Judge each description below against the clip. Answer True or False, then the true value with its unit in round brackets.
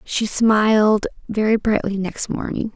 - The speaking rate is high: False (130 wpm)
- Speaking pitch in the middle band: False (215 Hz)